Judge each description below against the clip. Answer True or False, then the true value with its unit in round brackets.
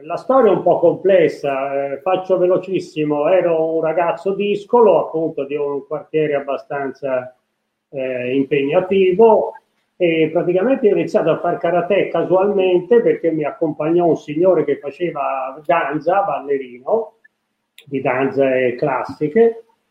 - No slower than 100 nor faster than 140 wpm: True (120 wpm)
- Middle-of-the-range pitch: True (165 Hz)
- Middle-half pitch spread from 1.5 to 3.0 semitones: False (4.8 semitones)